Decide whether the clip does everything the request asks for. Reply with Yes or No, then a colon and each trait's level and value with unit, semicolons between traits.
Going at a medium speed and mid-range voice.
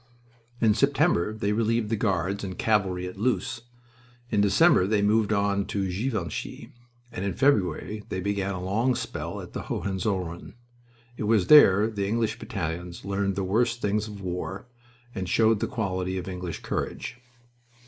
No: average, 160 wpm; low, 100 Hz